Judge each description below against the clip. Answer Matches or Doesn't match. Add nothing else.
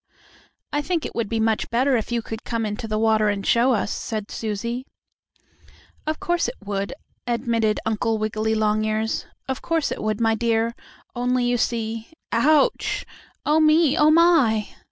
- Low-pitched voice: Doesn't match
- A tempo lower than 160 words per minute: Doesn't match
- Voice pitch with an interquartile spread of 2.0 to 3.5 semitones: Matches